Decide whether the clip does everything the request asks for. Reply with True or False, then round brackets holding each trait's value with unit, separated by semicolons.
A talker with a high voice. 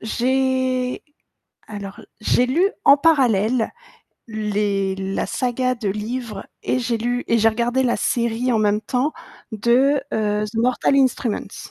True (235 Hz)